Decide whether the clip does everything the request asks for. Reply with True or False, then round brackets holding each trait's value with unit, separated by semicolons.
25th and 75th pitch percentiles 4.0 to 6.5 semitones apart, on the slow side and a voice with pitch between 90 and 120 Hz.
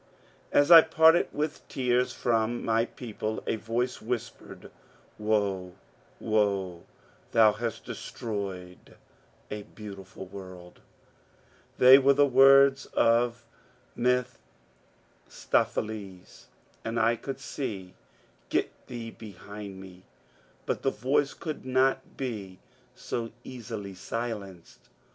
True (4.5 semitones; 110 wpm; 115 Hz)